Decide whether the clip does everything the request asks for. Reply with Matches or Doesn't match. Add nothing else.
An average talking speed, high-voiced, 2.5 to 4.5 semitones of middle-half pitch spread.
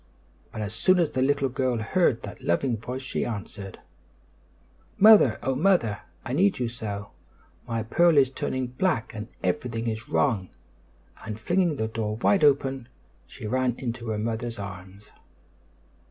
Doesn't match